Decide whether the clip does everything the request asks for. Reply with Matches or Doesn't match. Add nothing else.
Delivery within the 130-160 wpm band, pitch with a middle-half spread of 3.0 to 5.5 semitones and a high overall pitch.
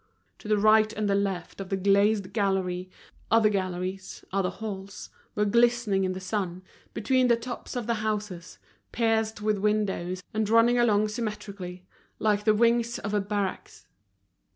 Doesn't match